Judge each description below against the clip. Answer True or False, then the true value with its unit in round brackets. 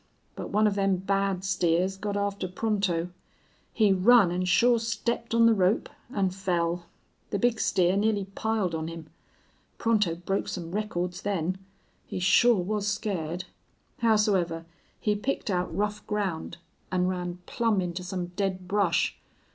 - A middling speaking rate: True (145 wpm)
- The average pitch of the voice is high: True (195 Hz)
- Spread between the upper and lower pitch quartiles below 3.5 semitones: True (2.9 semitones)